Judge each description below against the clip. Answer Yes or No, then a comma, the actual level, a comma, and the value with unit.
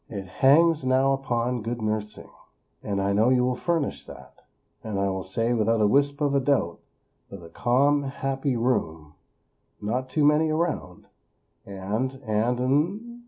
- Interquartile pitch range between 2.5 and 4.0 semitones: No, average, 5.0 semitones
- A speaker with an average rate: Yes, average, 160 wpm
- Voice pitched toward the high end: No, low, 125 Hz